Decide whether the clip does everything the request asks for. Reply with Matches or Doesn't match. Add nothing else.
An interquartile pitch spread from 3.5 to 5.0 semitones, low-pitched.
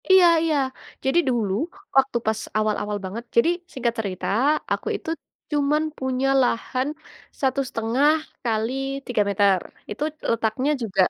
Doesn't match